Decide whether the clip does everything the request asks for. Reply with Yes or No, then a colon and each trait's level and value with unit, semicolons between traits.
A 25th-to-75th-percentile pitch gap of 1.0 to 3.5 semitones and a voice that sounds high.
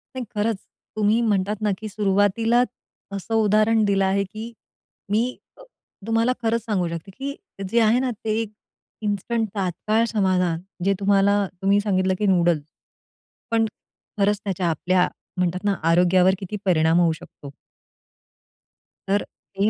Yes: average, 2.9 semitones; high, 200 Hz